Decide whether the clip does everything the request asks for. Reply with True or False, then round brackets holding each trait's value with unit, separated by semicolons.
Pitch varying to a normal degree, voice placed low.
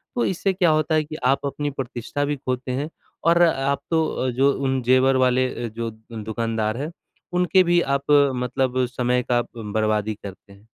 True (4.1 semitones; 130 Hz)